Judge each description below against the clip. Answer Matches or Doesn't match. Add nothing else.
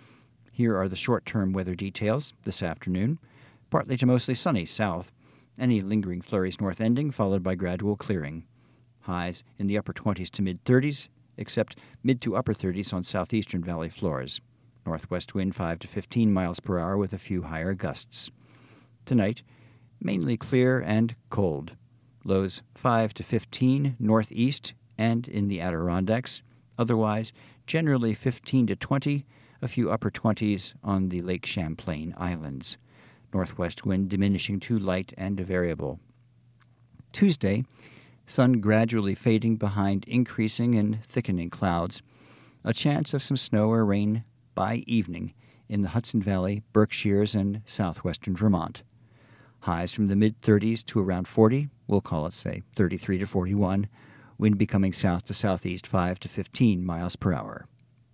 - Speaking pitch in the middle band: Doesn't match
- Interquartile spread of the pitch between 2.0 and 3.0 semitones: Doesn't match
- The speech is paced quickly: Doesn't match